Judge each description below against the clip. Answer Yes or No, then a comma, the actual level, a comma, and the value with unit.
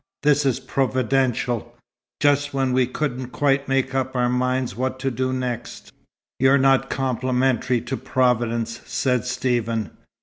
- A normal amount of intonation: No, narrow, 1.5 semitones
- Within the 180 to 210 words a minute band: No, slow, 135 wpm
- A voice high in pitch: No, low, 130 Hz